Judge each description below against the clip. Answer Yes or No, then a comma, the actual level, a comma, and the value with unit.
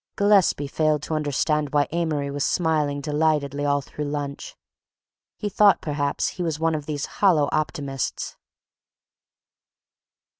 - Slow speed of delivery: Yes, slow, 125 wpm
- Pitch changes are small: Yes, narrow, 1.9 semitones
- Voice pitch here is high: No, medium, 150 Hz